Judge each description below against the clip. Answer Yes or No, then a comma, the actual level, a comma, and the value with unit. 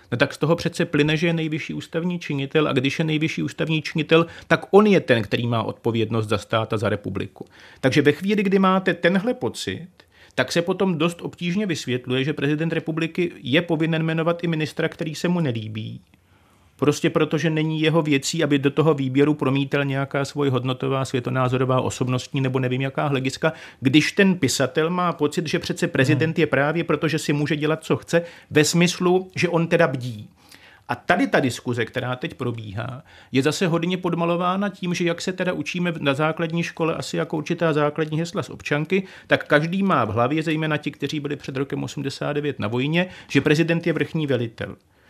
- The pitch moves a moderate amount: Yes, average, 4.0 semitones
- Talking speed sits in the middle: No, fast, 190 wpm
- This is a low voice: No, medium, 155 Hz